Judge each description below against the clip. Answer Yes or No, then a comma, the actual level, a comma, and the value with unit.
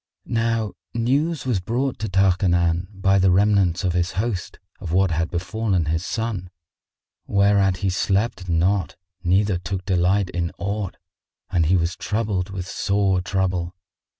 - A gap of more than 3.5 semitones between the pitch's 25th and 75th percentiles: No, narrow, 2.5 semitones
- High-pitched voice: No, very low, 95 Hz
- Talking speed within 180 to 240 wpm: No, average, 145 wpm